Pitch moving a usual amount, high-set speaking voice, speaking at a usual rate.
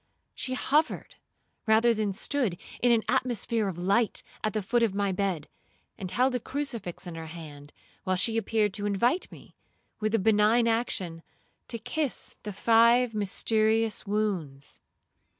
Yes: average, 3.7 semitones; high, 215 Hz; average, 150 wpm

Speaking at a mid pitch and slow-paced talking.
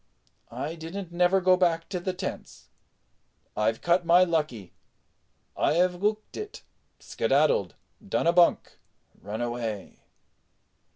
Yes: medium, 175 Hz; slow, 120 wpm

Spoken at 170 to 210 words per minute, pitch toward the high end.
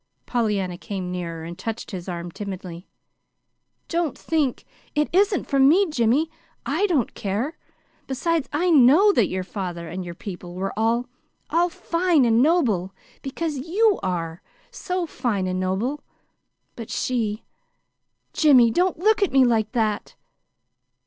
No: average, 140 wpm; high, 235 Hz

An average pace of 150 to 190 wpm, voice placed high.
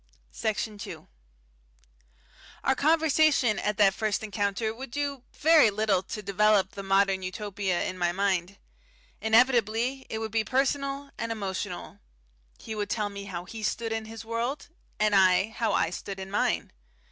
Yes: average, 155 wpm; high, 215 Hz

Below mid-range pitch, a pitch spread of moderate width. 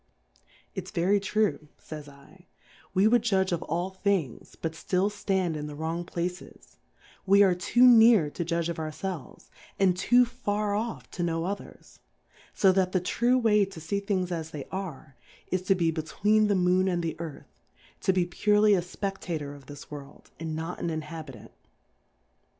No: medium, 180 Hz; average, 3.7 semitones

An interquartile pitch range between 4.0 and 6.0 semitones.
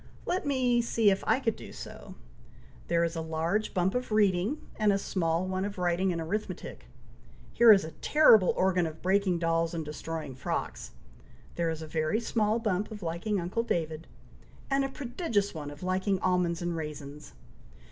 Yes: average, 4.4 semitones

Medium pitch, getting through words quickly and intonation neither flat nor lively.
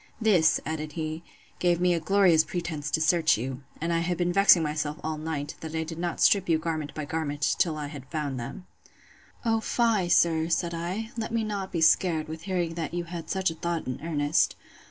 No: medium, 165 Hz; fast, 215 wpm; narrow, 2.2 semitones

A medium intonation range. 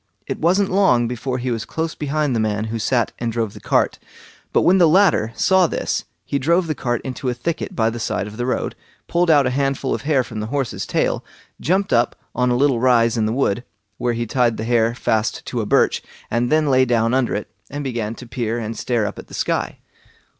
Yes: average, 3.8 semitones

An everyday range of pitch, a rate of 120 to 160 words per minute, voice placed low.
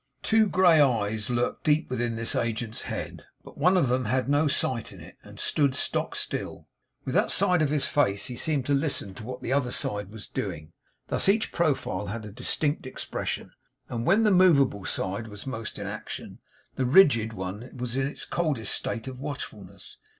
No: average, 4.8 semitones; average, 195 wpm; low, 130 Hz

